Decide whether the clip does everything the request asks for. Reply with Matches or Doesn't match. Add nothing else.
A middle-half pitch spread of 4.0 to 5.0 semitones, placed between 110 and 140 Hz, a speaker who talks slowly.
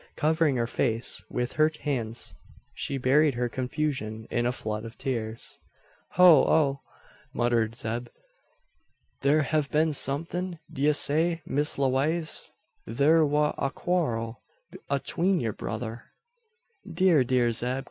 Matches